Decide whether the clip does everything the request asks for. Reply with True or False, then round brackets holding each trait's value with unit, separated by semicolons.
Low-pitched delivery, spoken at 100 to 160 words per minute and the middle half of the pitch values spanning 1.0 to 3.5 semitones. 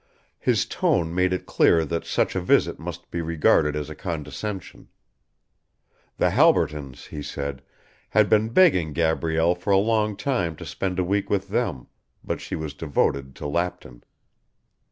False (85 Hz; 155 wpm; 4.5 semitones)